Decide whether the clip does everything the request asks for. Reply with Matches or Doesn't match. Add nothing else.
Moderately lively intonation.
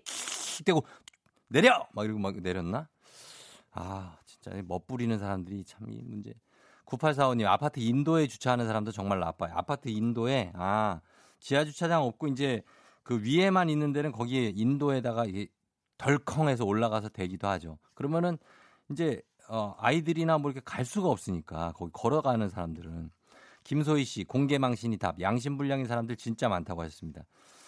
Doesn't match